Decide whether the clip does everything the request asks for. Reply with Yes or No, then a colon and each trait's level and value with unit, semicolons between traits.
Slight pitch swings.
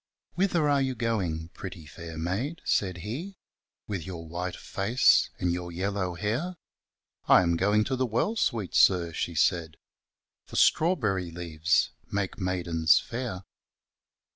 No: wide, 5.4 semitones